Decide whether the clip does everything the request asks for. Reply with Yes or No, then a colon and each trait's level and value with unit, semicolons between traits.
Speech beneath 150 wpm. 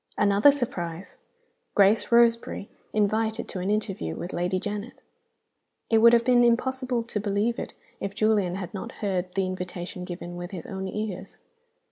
No: average, 160 wpm